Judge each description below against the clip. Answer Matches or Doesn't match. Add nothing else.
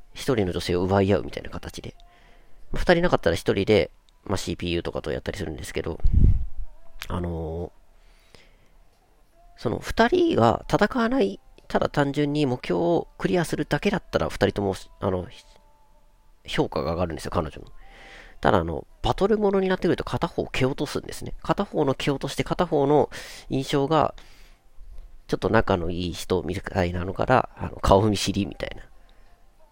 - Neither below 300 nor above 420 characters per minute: Matches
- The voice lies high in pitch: Doesn't match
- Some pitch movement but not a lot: Doesn't match